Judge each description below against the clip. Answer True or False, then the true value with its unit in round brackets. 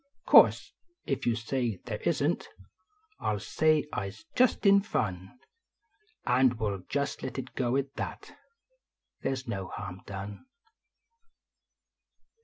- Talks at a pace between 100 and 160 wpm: True (140 wpm)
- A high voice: False (125 Hz)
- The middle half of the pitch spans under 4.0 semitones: False (5.1 semitones)